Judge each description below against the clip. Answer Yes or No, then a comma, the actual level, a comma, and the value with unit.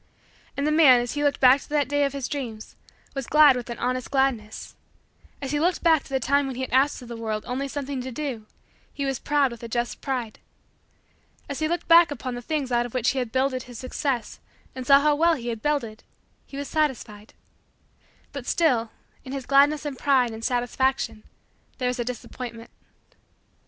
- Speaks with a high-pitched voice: Yes, very high, 265 Hz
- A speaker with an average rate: No, fast, 210 wpm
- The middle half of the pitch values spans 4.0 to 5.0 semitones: No, average, 2.9 semitones